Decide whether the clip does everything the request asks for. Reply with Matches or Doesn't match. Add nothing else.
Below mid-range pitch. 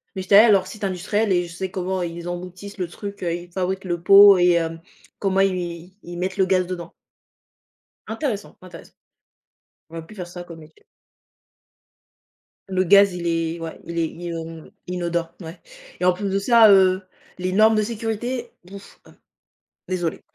Doesn't match